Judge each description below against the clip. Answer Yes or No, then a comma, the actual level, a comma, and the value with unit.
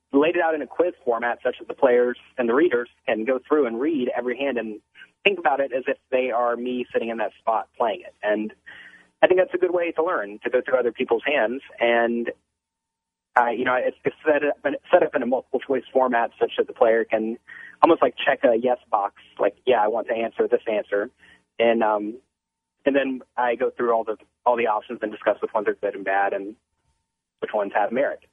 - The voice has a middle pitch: No, low, 120 Hz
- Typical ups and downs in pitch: Yes, average, 3.9 semitones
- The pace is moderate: No, fast, 235 wpm